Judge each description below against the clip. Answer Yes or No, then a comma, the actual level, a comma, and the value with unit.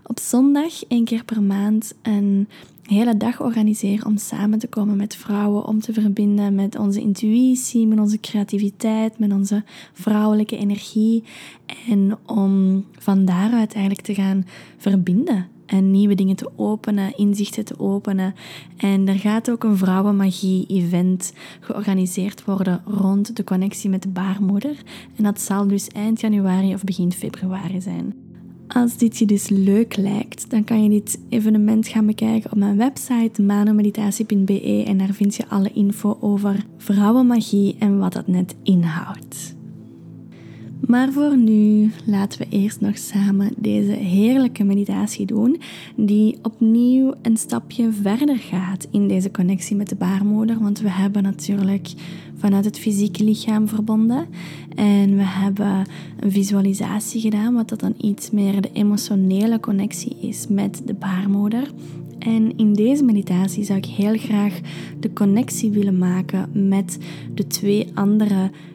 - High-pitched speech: Yes, high, 205 Hz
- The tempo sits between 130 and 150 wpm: Yes, average, 145 wpm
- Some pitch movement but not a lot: No, narrow, 1.9 semitones